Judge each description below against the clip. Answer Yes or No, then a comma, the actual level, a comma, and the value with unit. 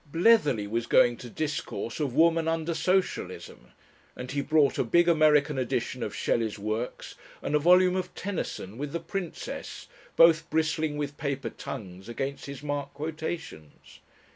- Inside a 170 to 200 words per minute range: No, average, 150 wpm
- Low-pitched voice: No, medium, 150 Hz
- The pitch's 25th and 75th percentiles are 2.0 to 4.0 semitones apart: No, average, 4.7 semitones